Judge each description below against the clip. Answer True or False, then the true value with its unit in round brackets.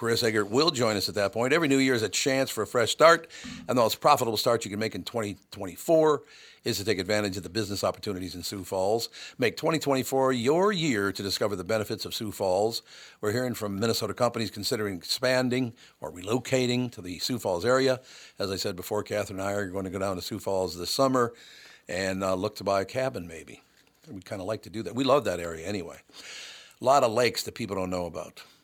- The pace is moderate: False (230 wpm)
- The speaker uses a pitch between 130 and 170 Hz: False (105 Hz)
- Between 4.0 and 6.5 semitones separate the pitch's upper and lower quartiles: True (4.5 semitones)